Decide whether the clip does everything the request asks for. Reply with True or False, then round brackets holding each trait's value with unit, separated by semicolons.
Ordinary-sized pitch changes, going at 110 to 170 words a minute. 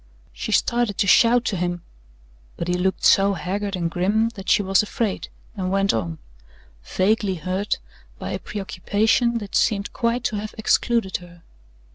True (3.1 semitones; 160 wpm)